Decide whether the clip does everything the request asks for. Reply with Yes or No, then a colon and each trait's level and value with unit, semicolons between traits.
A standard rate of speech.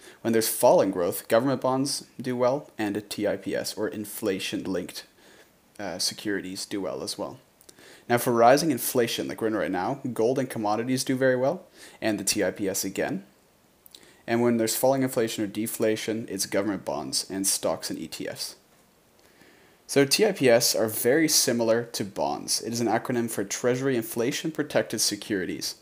Yes: average, 160 wpm